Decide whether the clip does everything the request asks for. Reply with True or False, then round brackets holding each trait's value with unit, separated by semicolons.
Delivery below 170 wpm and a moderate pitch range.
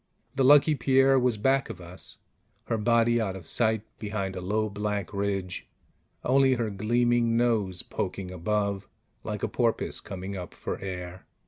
True (155 wpm; 3.9 semitones)